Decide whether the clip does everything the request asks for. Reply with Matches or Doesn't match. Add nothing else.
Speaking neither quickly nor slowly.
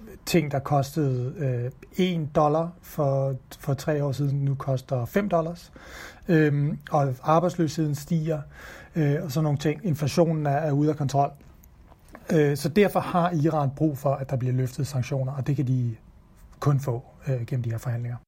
Matches